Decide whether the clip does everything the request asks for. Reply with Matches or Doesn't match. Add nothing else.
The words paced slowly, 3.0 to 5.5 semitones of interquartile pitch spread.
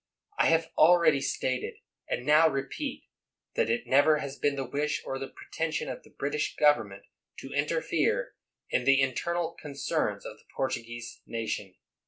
Doesn't match